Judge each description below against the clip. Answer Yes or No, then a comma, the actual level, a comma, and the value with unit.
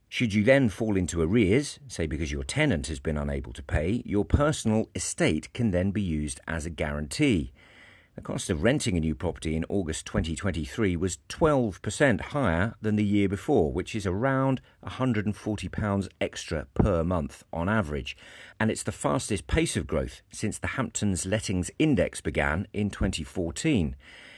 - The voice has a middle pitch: No, very low, 95 Hz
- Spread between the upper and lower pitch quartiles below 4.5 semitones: No, average, 5.2 semitones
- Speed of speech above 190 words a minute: No, average, 160 wpm